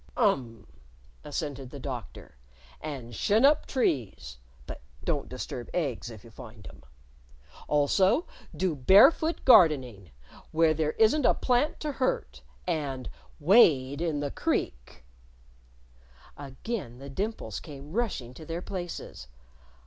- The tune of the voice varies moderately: No, wide, 7.3 semitones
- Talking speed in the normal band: No, slow, 120 wpm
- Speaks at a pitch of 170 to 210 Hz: No, medium, 145 Hz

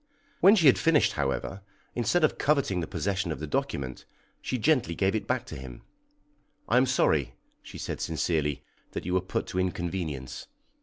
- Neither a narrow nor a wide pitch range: No, wide, 8.6 semitones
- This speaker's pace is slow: No, average, 175 wpm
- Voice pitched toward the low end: Yes, very low, 95 Hz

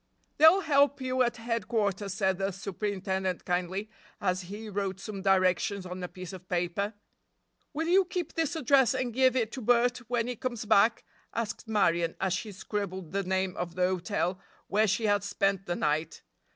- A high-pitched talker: Yes, high, 200 Hz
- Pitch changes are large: No, average, 4.2 semitones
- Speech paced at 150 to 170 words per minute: No, average, 180 wpm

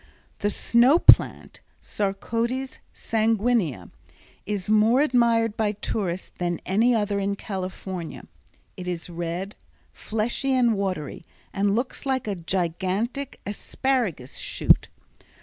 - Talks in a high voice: Yes, high, 205 Hz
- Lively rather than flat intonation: No, average, 4.1 semitones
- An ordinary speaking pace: No, slow, 110 wpm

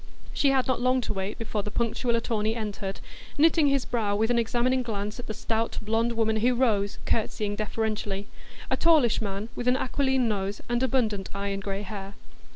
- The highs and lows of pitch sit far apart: No, average, 3.2 semitones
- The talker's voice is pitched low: No, high, 225 Hz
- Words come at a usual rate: Yes, average, 180 wpm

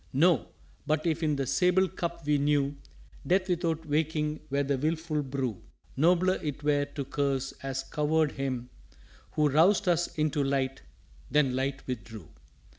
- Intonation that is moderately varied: Yes, average, 3.0 semitones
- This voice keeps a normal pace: Yes, average, 155 wpm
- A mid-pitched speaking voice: Yes, medium, 150 Hz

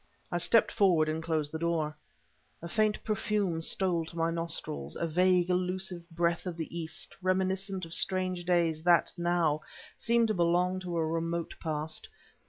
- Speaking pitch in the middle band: Yes, medium, 170 Hz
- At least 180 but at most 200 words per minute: No, average, 165 wpm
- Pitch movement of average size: No, narrow, 2.2 semitones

